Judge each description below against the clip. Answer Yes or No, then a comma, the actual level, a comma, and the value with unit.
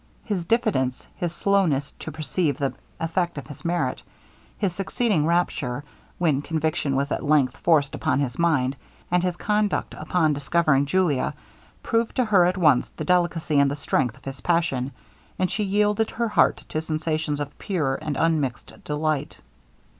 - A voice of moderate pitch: Yes, medium, 160 Hz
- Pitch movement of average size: Yes, average, 4.2 semitones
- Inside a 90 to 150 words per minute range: No, average, 160 wpm